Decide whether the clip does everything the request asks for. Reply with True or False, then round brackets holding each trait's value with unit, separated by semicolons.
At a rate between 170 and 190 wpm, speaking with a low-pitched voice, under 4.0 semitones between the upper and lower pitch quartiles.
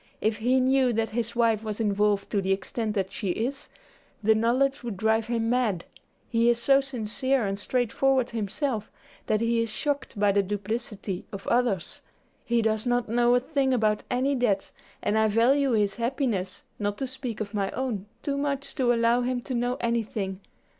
False (185 wpm; 230 Hz; 3.1 semitones)